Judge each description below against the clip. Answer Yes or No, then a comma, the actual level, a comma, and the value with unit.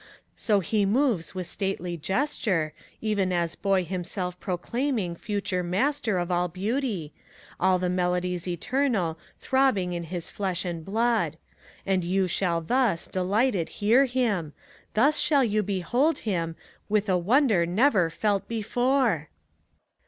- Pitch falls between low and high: No, high, 195 Hz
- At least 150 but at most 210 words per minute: No, slow, 135 wpm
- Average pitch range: Yes, average, 4.6 semitones